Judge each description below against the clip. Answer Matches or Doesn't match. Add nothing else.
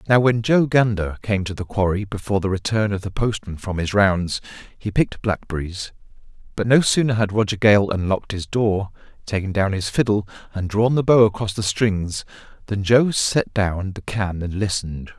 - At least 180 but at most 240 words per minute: Matches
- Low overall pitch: Matches